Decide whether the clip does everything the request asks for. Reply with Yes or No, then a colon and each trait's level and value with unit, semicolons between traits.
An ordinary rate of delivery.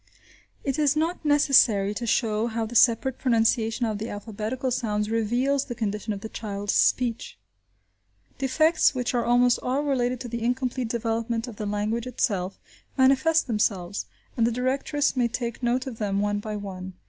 Yes: average, 170 wpm